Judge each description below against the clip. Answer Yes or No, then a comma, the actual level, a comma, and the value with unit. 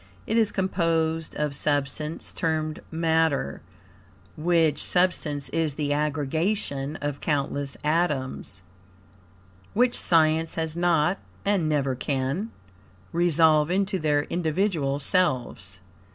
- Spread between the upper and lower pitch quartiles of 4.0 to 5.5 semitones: No, average, 3.1 semitones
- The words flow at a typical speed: No, slow, 100 wpm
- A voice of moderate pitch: Yes, medium, 155 Hz